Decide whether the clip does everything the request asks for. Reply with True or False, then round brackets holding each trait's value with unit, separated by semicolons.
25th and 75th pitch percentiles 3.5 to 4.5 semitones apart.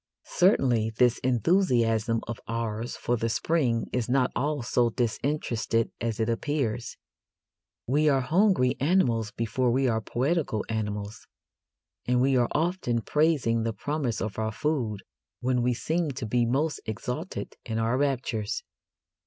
True (4.0 semitones)